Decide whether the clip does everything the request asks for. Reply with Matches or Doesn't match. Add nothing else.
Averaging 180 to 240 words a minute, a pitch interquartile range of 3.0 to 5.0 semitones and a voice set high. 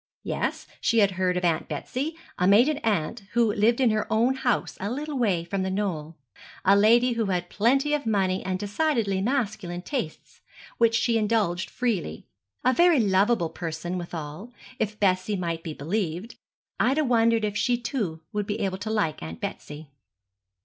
Doesn't match